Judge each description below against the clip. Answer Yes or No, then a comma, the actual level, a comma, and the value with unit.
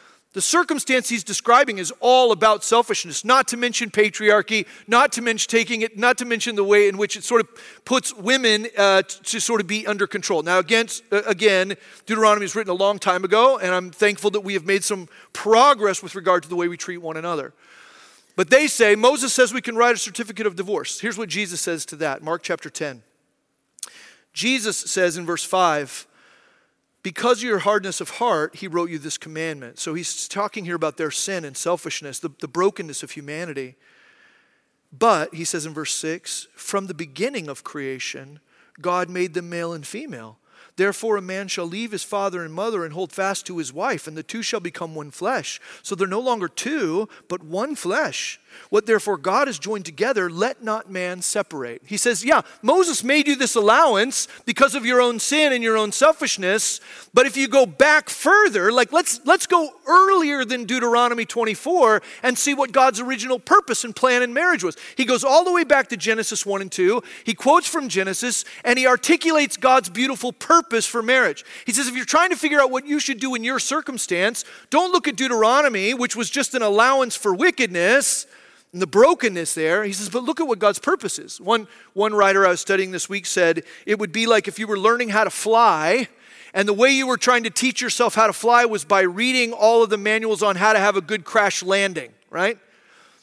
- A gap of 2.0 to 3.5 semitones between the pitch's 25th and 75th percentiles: No, average, 5.1 semitones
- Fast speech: Yes, fast, 210 wpm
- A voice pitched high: Yes, high, 215 Hz